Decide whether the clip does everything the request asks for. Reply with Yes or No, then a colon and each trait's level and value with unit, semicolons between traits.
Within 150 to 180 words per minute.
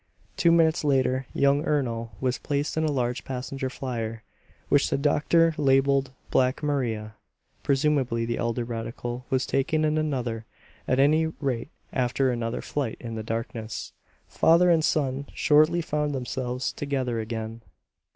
No: average, 140 wpm